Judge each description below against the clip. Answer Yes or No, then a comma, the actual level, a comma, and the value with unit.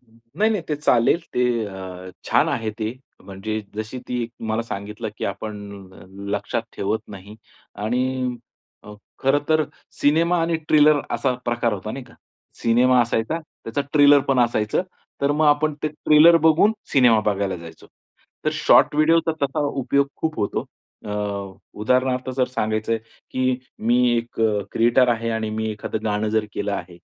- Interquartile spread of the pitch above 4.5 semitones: Yes, average, 4.9 semitones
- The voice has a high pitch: No, low, 120 Hz